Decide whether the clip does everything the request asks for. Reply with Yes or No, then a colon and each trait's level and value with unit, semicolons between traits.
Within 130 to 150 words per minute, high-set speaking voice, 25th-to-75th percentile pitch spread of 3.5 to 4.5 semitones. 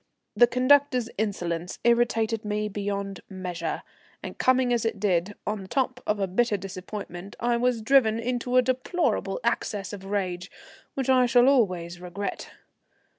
Yes: average, 145 wpm; high, 215 Hz; average, 4.1 semitones